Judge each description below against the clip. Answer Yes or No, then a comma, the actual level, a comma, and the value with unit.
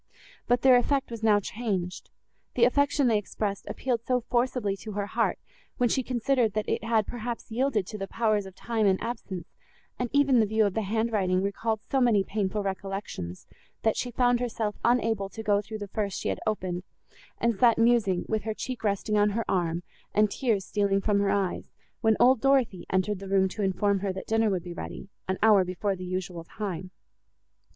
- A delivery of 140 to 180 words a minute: No, average, 200 wpm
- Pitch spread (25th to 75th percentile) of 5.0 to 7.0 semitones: No, average, 3.2 semitones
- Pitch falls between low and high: No, high, 210 Hz